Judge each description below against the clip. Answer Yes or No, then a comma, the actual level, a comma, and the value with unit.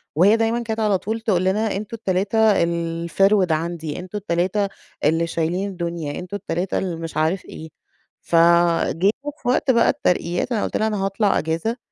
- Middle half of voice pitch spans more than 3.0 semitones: Yes, average, 4.1 semitones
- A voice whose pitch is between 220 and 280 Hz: No, medium, 185 Hz